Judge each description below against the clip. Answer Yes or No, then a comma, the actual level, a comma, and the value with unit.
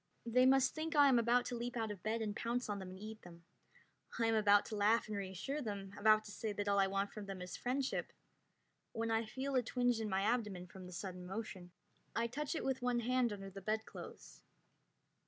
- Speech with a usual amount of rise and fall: Yes, average, 3.7 semitones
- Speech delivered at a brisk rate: Yes, fast, 230 wpm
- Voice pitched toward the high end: Yes, high, 220 Hz